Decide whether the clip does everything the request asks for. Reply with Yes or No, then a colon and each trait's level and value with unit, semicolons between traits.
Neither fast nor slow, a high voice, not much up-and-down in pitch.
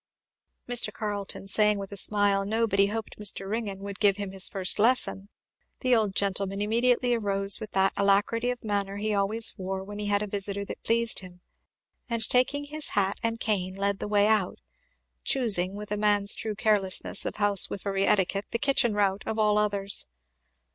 Yes: average, 185 wpm; high, 205 Hz; narrow, 1.9 semitones